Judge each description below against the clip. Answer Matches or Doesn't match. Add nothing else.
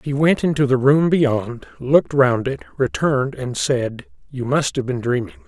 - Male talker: Matches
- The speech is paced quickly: Doesn't match